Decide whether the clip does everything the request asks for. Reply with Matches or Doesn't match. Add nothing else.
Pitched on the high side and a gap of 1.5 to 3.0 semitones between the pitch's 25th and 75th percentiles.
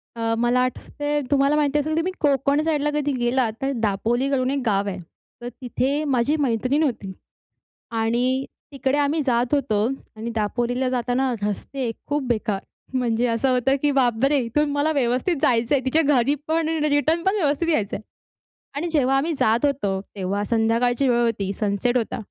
Doesn't match